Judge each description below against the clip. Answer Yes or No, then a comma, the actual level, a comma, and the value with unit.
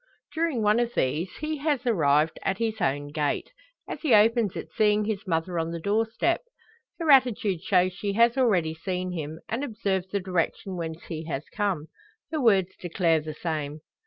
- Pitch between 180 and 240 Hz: Yes, high, 190 Hz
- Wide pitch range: Yes, wide, 5.7 semitones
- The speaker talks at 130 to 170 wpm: No, average, 185 wpm